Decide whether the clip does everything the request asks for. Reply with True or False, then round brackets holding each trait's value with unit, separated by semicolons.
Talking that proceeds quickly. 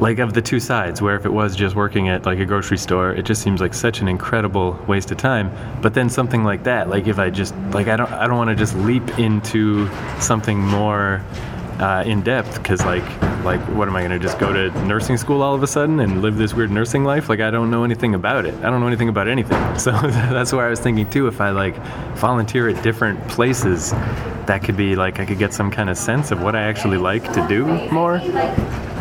True (245 wpm)